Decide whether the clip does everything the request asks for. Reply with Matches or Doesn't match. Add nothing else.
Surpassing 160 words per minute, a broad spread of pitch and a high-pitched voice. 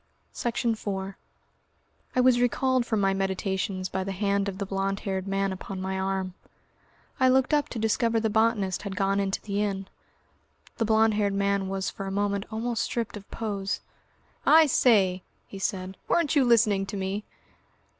Doesn't match